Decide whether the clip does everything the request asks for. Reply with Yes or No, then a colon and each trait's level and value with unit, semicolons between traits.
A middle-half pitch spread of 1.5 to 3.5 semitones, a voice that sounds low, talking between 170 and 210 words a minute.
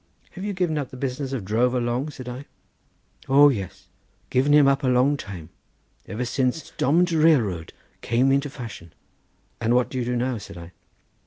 Yes: average, 3.2 semitones; low, 130 Hz; average, 180 wpm